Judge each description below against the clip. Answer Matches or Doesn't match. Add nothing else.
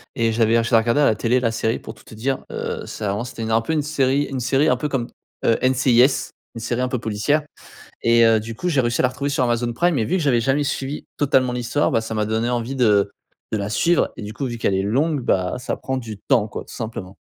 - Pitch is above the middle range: Doesn't match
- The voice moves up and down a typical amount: Matches